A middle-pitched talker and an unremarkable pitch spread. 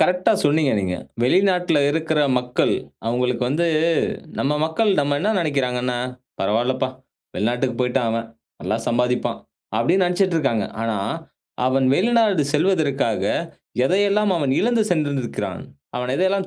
No: medium, 145 Hz; wide, 6.4 semitones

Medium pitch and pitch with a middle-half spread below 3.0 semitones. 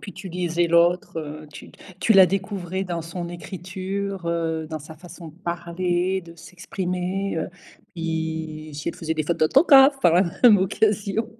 Yes: medium, 175 Hz; narrow, 2.6 semitones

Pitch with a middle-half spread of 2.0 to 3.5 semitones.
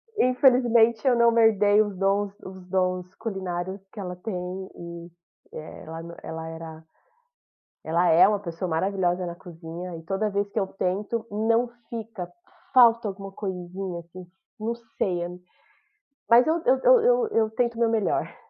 No: average, 4.3 semitones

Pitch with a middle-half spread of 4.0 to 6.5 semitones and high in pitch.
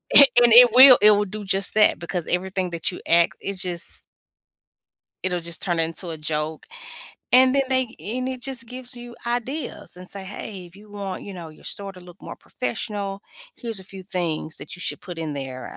Yes: average, 5.2 semitones; high, 195 Hz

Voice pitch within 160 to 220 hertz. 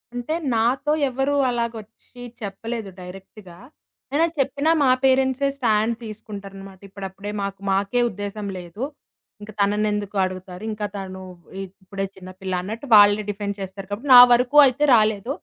Yes: high, 210 Hz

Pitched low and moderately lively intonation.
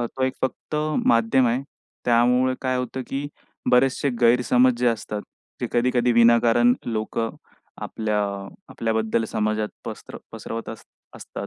No: low, 120 Hz; narrow, 1.9 semitones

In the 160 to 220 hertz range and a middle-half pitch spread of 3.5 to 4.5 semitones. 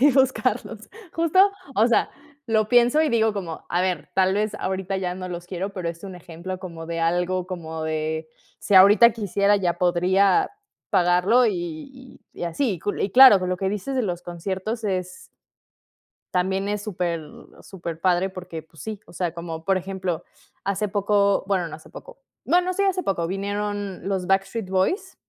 No: high, 190 Hz; average, 3.0 semitones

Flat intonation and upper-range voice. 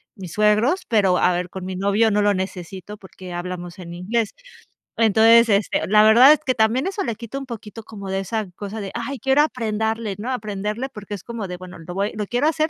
No: average, 3.4 semitones; high, 210 Hz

